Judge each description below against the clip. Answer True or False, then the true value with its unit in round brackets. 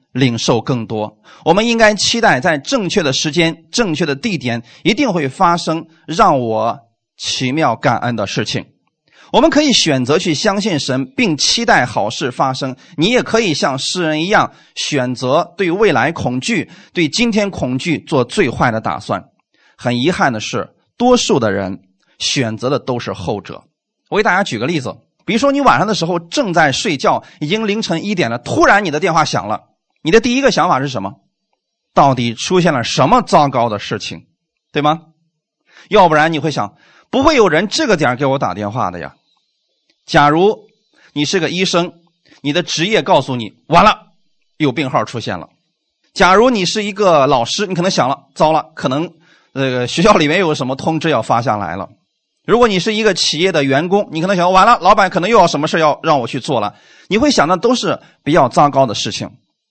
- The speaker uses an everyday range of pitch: False (6.9 semitones)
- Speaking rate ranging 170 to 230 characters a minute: False (275 characters per minute)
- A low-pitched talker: False (160 Hz)